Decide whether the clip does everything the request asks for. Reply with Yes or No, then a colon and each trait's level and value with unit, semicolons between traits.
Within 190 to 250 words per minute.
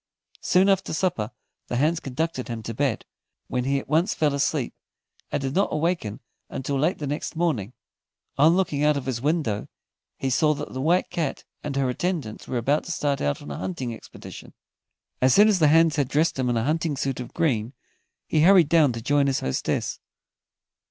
Yes: average, 200 wpm